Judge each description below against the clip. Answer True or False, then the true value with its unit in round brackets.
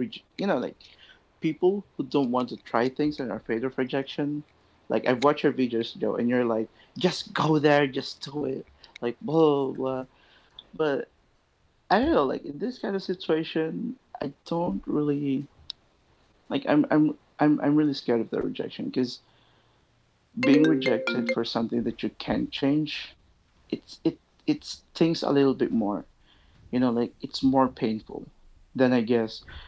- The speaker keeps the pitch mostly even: False (4.0 semitones)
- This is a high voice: False (135 Hz)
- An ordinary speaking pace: True (170 wpm)